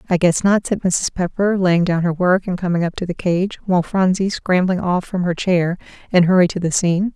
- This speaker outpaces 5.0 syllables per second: Yes, 5.4 syllables/s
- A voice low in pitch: No, medium, 180 Hz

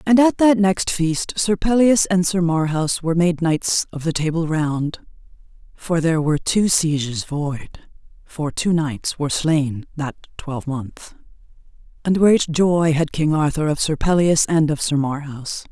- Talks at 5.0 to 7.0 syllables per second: No, 4.3 syllables/s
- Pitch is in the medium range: Yes, medium, 160 Hz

